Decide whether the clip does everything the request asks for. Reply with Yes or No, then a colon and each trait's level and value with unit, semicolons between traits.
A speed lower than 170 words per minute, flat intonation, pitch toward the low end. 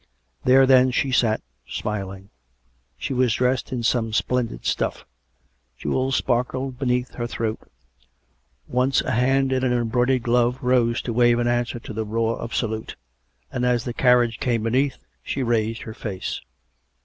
Yes: average, 155 wpm; narrow, 1.9 semitones; low, 120 Hz